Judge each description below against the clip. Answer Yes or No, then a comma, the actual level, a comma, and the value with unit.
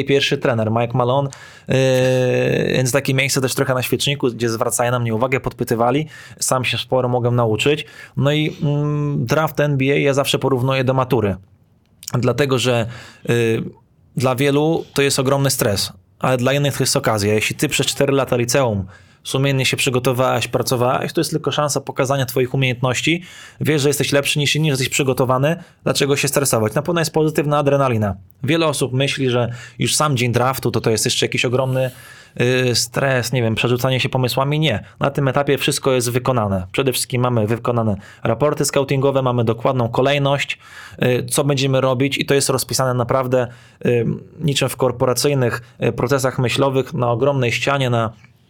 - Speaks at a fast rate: Yes, fast, 165 wpm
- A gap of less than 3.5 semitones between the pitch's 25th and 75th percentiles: Yes, narrow, 2.4 semitones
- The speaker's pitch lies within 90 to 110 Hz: No, low, 130 Hz